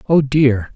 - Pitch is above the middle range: No, low, 135 Hz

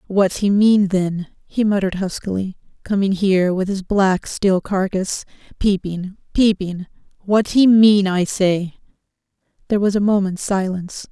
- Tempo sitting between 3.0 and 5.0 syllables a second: Yes, 4.6 syllables/s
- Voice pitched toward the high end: Yes, high, 195 Hz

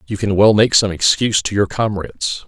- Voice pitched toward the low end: Yes, low, 100 Hz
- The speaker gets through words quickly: Yes, fast, 220 wpm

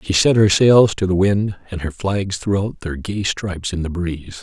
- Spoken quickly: Yes, fast, 245 wpm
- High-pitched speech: No, very low, 95 Hz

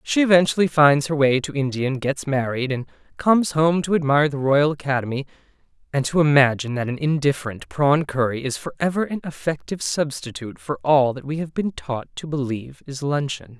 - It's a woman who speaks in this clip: No, male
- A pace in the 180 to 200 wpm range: Yes, average, 190 wpm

